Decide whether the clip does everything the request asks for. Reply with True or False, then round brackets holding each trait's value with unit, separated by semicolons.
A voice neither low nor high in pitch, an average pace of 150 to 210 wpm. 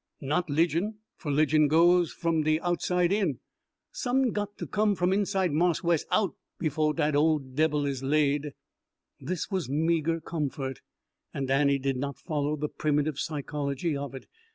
True (155 Hz; 155 wpm)